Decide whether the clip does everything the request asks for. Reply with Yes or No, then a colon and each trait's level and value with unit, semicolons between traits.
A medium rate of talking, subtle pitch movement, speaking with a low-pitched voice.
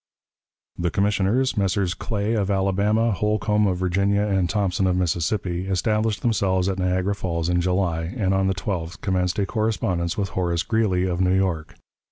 Yes: average, 165 wpm; narrow, 2.2 semitones; very low, 95 Hz